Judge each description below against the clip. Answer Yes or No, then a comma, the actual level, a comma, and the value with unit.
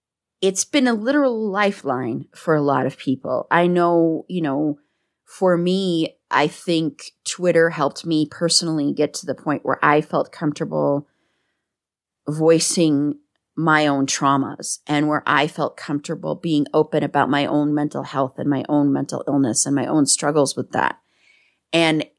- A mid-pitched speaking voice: Yes, medium, 150 Hz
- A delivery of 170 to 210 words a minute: No, average, 155 wpm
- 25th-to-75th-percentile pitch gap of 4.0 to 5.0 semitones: No, narrow, 2.6 semitones